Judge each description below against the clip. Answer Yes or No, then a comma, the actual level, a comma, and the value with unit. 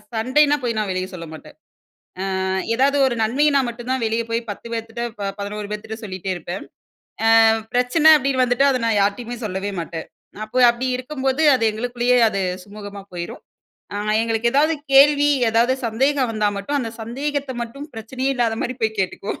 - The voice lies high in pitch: Yes, high, 235 Hz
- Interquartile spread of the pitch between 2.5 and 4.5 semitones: Yes, average, 3.7 semitones